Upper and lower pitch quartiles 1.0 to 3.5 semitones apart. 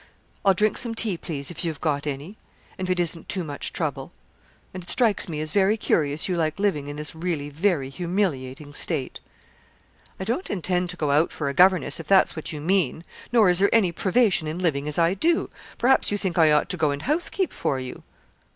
No: average, 4.5 semitones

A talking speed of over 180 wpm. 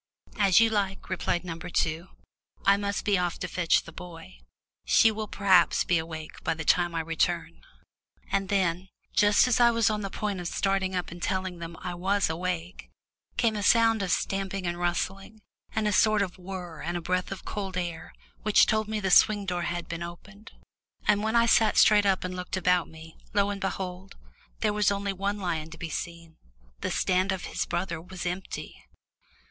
Yes: average, 195 wpm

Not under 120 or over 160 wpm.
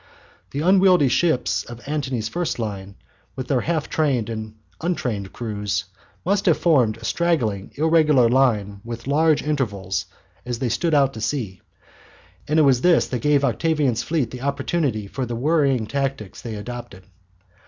Yes: average, 155 wpm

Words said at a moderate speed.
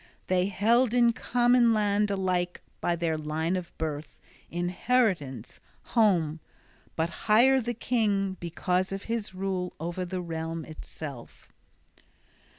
No: slow, 120 wpm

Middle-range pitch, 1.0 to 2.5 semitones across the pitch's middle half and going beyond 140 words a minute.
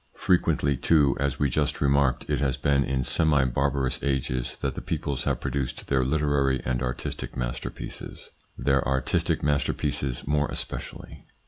No: very low, 70 Hz; narrow, 1.7 semitones; average, 150 wpm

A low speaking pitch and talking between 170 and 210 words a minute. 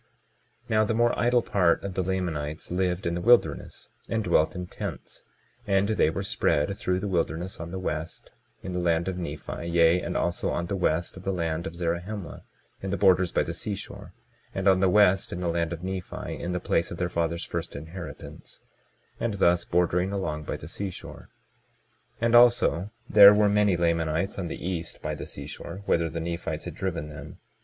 Yes: very low, 90 Hz; average, 200 wpm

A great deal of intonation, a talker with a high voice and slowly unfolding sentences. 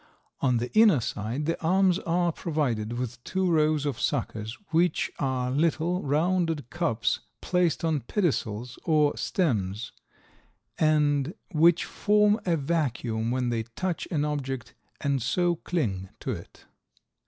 No: wide, 5.9 semitones; medium, 150 Hz; slow, 130 wpm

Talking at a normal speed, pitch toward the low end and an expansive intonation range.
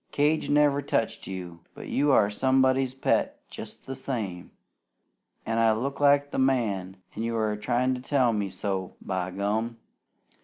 No: average, 160 wpm; low, 115 Hz; average, 4.7 semitones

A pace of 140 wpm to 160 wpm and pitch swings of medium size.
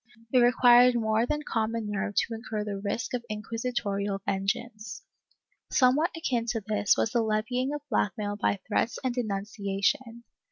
Yes: average, 150 wpm; average, 3.0 semitones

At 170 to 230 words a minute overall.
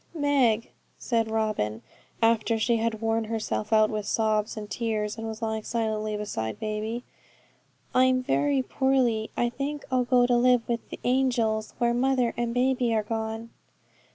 No: average, 155 wpm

